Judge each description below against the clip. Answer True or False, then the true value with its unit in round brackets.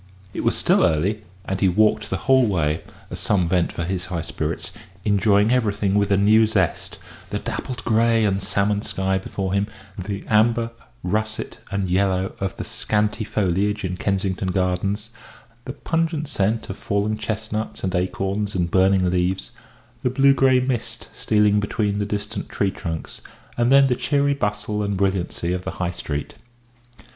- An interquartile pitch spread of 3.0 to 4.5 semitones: False (2.6 semitones)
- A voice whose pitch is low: True (100 Hz)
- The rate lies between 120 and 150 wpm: False (165 wpm)